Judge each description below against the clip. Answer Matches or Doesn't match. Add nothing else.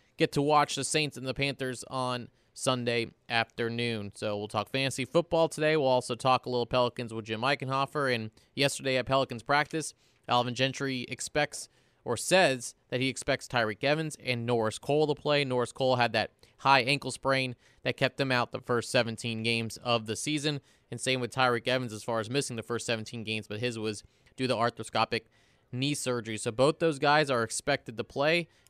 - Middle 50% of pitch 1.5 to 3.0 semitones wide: Matches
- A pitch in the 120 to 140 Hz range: Matches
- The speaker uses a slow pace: Doesn't match